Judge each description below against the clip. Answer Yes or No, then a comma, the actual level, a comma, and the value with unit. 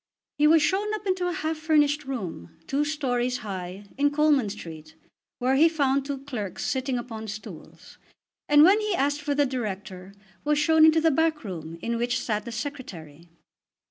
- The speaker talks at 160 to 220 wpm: Yes, average, 175 wpm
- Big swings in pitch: Yes, wide, 6.2 semitones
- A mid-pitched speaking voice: No, very high, 270 Hz